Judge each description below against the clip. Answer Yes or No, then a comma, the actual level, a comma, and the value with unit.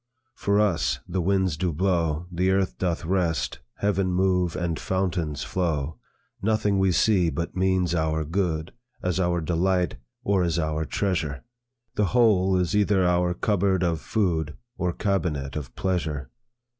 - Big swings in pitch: No, average, 2.8 semitones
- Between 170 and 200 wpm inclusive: No, average, 145 wpm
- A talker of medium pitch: No, very low, 90 Hz